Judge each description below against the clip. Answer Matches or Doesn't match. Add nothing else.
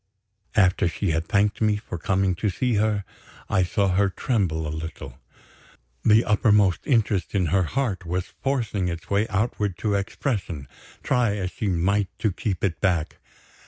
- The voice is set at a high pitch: Doesn't match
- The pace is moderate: Matches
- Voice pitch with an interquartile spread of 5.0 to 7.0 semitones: Doesn't match